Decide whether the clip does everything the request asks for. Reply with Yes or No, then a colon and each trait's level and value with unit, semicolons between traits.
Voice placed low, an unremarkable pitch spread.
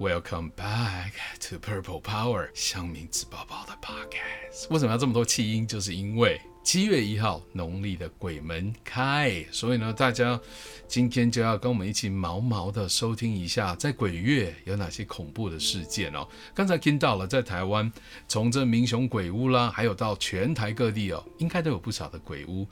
Yes: low, 110 Hz; average, 4.6 semitones